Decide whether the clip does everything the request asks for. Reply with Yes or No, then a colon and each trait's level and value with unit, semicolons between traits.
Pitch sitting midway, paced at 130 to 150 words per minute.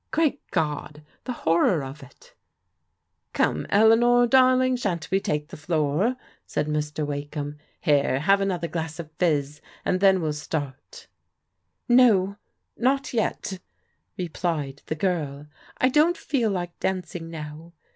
Yes: medium, 170 Hz; average, 140 wpm